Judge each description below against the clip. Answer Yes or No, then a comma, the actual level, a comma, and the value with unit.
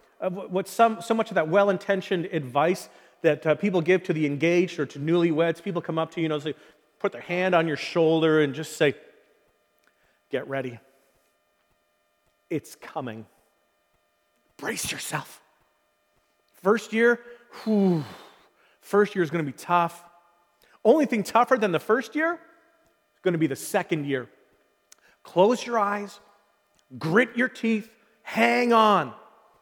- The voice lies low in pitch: No, medium, 175 Hz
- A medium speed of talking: Yes, average, 150 wpm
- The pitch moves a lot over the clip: Yes, wide, 6.2 semitones